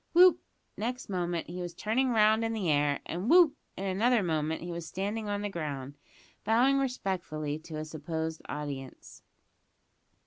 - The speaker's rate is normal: Yes, average, 160 wpm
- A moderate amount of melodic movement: No, wide, 6.1 semitones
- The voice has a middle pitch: Yes, medium, 180 Hz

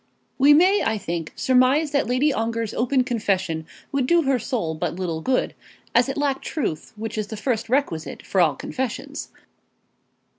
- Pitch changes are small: No, average, 5.3 semitones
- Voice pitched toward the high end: Yes, high, 240 Hz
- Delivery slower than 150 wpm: No, average, 170 wpm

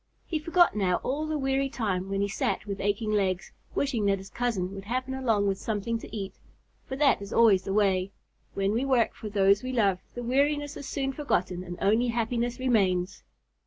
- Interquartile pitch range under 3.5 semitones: No, average, 4.8 semitones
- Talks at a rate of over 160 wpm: Yes, average, 200 wpm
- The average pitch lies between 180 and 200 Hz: No, high, 220 Hz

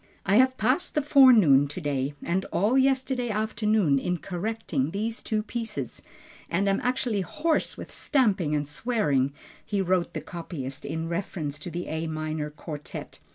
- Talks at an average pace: Yes, average, 155 wpm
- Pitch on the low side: No, medium, 185 Hz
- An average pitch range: No, wide, 6.8 semitones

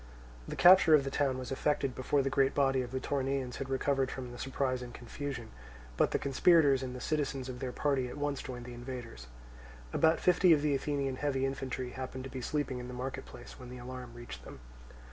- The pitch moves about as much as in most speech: No, narrow, 1.9 semitones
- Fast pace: Yes, fast, 220 wpm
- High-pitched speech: No, low, 130 Hz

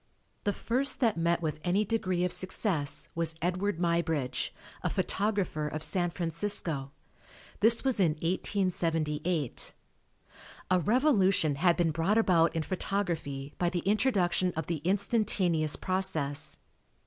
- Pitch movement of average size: Yes, average, 3.7 semitones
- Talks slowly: Yes, slow, 125 wpm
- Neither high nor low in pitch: Yes, medium, 175 Hz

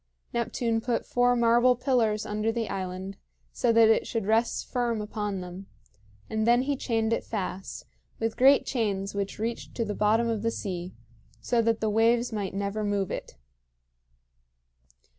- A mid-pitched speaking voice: No, high, 225 Hz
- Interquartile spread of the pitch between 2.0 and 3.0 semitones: Yes, narrow, 2.5 semitones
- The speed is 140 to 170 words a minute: Yes, average, 160 wpm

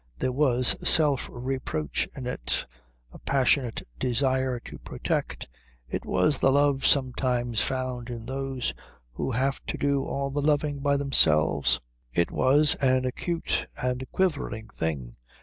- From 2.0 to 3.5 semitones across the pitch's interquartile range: Yes, narrow, 2.5 semitones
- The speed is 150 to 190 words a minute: No, slow, 135 wpm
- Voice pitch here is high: No, low, 130 Hz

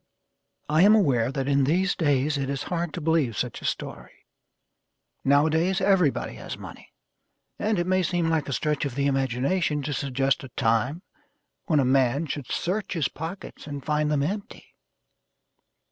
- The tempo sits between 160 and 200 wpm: Yes, average, 165 wpm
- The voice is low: No, medium, 150 Hz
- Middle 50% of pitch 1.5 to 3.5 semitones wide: No, average, 4.1 semitones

